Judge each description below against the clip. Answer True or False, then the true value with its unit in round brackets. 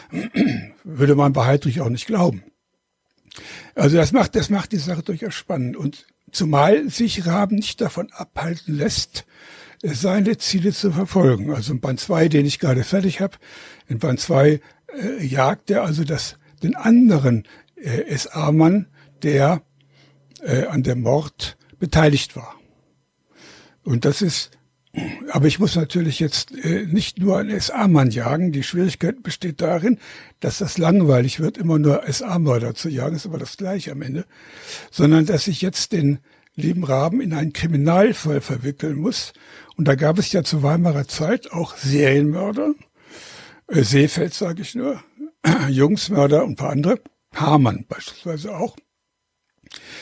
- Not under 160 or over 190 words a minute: False (150 wpm)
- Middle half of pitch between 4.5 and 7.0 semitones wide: True (5.0 semitones)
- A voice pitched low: False (160 Hz)